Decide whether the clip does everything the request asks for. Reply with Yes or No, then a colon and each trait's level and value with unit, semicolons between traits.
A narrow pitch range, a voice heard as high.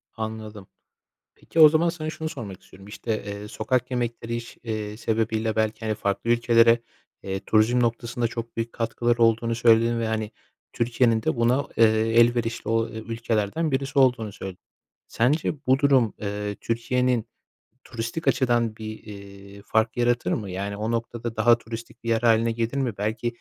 No: narrow, 1.7 semitones; low, 115 Hz